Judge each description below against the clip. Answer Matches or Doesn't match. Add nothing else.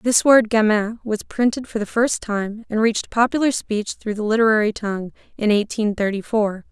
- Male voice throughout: Doesn't match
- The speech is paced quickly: Doesn't match